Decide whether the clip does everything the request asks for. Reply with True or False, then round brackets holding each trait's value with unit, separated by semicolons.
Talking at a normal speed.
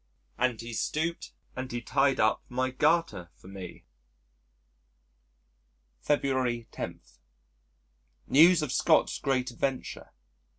False (100 wpm)